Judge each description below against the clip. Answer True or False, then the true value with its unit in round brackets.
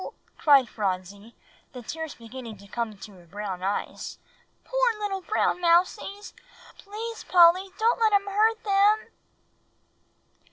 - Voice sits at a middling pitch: False (340 Hz)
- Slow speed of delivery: True (125 wpm)